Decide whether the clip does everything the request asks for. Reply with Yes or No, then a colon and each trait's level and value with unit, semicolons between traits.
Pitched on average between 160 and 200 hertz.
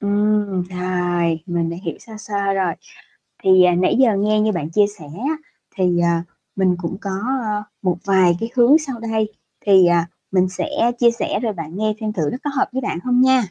Yes: high, 195 Hz